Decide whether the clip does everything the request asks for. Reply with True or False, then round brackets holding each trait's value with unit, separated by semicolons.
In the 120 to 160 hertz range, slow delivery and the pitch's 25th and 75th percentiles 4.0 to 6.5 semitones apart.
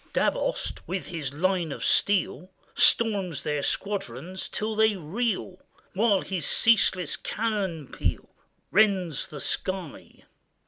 False (185 Hz; 110 wpm; 4.3 semitones)